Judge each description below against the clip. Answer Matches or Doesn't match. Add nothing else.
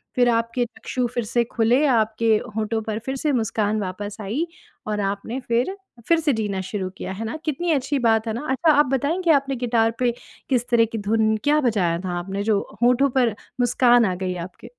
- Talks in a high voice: Matches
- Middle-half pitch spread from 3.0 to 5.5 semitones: Matches